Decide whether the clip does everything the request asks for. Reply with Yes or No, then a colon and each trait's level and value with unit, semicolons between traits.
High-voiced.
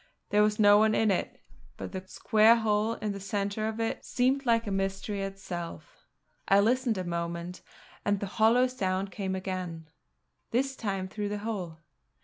Yes: high, 205 Hz